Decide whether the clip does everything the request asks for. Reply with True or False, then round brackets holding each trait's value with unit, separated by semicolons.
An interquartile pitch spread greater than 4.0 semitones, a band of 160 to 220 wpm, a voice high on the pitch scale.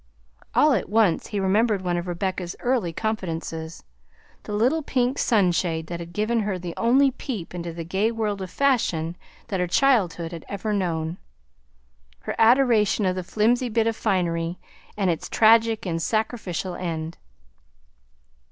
False (4.7 semitones; 150 wpm; 195 Hz)